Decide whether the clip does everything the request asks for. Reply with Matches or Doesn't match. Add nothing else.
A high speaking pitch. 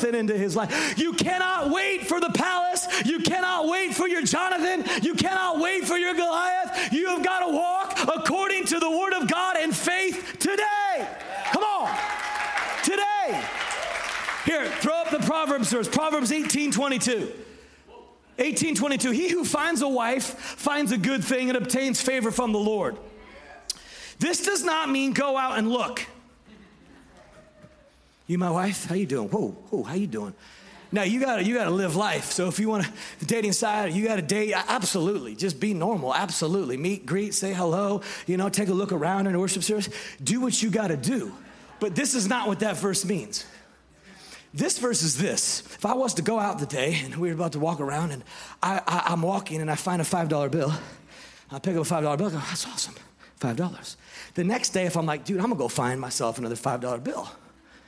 Matches